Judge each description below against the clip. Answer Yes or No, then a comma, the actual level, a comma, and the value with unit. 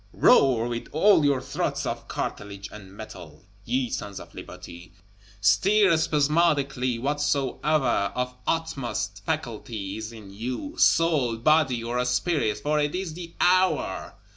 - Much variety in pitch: Yes, wide, 6.1 semitones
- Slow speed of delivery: Yes, slow, 130 wpm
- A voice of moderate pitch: No, low, 125 Hz